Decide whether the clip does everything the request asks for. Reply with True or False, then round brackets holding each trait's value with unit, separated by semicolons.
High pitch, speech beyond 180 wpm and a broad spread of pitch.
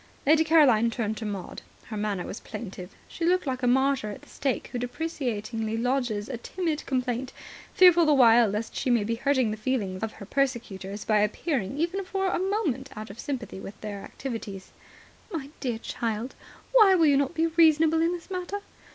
True (250 Hz; 190 wpm; 6.6 semitones)